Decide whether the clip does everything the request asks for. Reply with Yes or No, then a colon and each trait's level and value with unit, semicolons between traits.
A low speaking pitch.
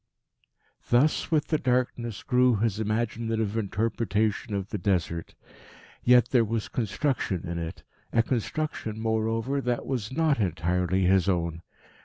Yes: low, 110 Hz